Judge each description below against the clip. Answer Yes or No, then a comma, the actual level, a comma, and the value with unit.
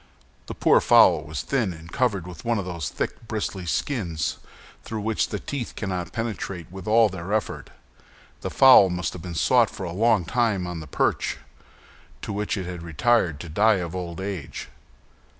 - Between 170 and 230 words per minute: Yes, average, 185 wpm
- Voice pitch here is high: No, very low, 95 Hz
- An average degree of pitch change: Yes, average, 4.5 semitones